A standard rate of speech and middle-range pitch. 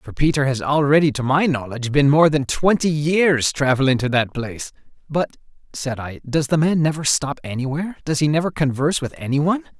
Yes: average, 190 wpm; medium, 145 Hz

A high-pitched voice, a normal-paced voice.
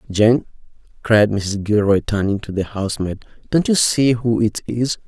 No: low, 110 Hz; average, 165 wpm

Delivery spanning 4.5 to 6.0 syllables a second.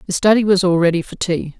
No: 6.3 syllables/s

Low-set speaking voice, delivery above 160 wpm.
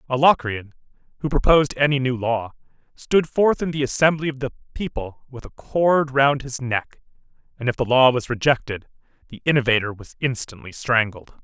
Yes: low, 130 Hz; average, 170 wpm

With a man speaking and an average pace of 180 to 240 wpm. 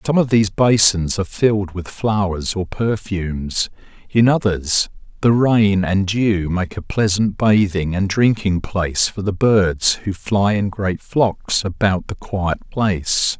No: male; average, 155 wpm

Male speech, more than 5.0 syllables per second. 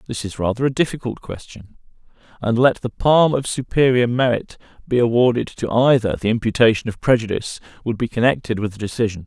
Yes: male; 5.9 syllables/s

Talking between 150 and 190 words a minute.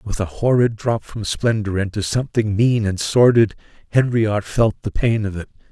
Yes: average, 180 wpm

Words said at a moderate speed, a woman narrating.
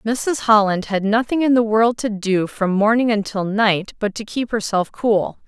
Yes: average, 195 wpm; female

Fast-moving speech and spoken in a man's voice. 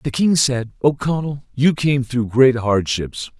No: average, 175 wpm; male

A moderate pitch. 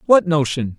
Yes: medium, 145 Hz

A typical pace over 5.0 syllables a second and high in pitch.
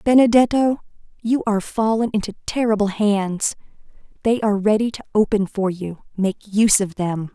Yes: 5.2 syllables/s; high, 210 Hz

